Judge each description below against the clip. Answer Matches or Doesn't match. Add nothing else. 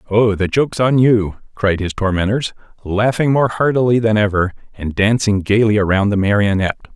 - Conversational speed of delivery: Matches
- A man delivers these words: Matches